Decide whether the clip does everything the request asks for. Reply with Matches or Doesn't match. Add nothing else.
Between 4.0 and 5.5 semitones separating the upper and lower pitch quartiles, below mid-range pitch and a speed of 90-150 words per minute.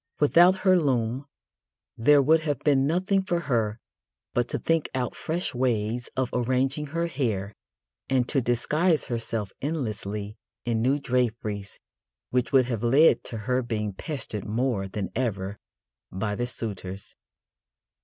Matches